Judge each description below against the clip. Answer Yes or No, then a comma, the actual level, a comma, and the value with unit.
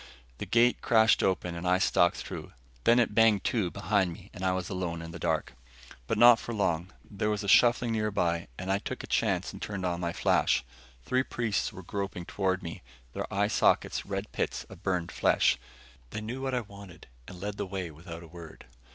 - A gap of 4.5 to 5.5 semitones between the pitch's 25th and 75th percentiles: No, average, 3.5 semitones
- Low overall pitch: Yes, very low, 95 Hz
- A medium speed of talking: No, fast, 210 wpm